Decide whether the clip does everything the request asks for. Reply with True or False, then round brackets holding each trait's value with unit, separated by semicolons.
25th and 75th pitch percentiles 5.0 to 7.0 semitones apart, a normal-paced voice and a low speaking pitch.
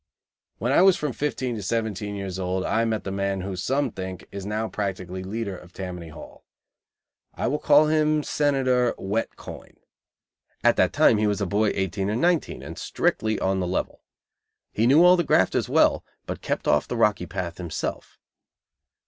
True (5.4 semitones; 180 wpm; 105 Hz)